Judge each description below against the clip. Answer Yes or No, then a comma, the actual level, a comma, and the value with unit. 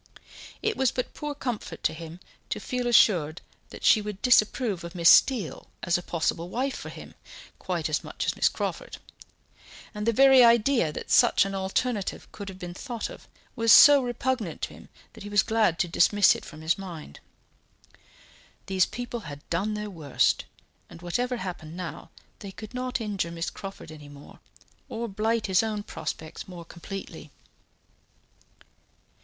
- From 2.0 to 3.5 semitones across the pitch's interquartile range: No, wide, 5.6 semitones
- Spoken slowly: No, average, 170 wpm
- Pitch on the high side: Yes, high, 200 Hz